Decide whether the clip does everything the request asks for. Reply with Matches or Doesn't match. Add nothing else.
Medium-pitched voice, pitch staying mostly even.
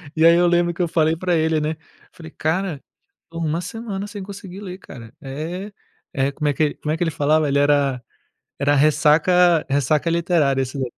Doesn't match